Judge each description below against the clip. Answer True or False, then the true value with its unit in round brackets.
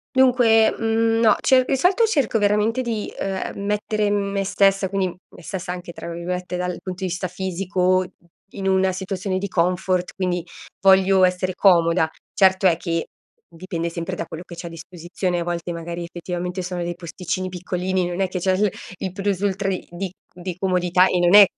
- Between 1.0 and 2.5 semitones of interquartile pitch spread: True (1.9 semitones)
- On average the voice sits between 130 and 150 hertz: False (185 Hz)